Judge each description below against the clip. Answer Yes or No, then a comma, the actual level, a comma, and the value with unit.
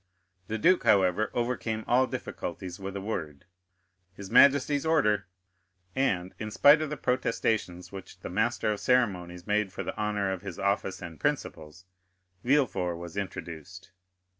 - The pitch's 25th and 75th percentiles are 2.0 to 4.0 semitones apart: No, average, 4.5 semitones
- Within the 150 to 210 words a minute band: No, average, 140 wpm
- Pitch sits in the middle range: No, low, 100 Hz